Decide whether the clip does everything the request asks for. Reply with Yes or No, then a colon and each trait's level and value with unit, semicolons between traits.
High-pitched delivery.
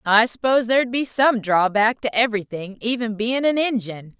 Yes: high, 225 Hz